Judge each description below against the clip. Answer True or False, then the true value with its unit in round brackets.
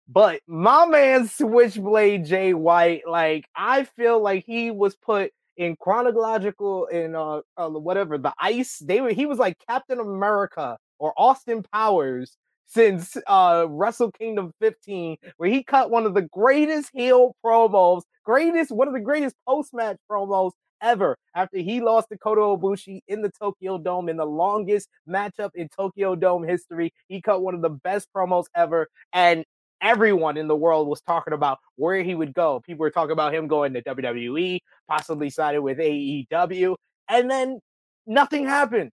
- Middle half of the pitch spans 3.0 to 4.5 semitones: False (5.3 semitones)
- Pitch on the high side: True (195 Hz)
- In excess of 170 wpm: False (165 wpm)